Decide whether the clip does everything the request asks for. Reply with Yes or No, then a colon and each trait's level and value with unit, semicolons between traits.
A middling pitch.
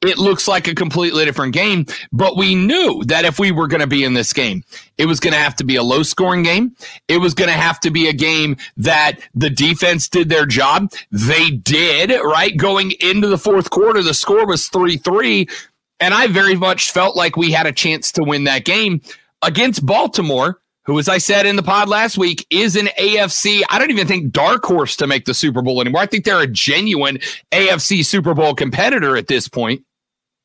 Yes: medium, 175 Hz